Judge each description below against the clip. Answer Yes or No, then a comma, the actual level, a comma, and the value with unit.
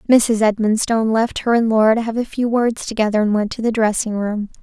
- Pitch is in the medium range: No, high, 220 Hz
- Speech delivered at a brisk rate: Yes, fast, 235 wpm